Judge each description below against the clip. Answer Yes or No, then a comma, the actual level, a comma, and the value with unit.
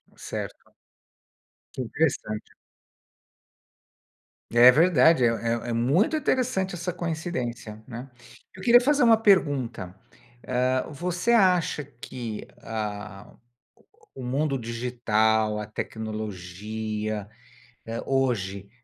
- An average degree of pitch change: No, wide, 7.1 semitones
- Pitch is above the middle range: No, low, 125 Hz